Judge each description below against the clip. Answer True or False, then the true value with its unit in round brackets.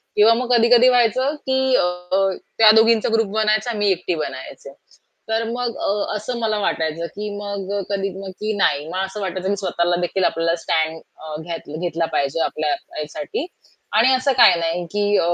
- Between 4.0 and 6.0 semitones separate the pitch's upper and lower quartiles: True (5.0 semitones)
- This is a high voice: True (205 Hz)